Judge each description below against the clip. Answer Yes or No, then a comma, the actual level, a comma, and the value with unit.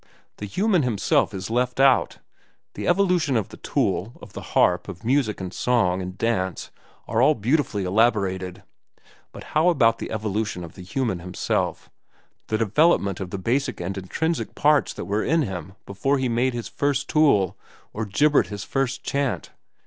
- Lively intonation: Yes, wide, 6.3 semitones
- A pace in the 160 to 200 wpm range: Yes, average, 170 wpm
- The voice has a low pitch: Yes, low, 115 Hz